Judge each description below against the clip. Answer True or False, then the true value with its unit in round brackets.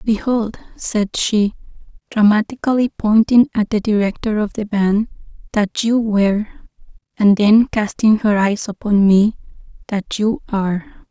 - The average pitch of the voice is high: True (210 Hz)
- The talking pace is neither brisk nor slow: False (130 wpm)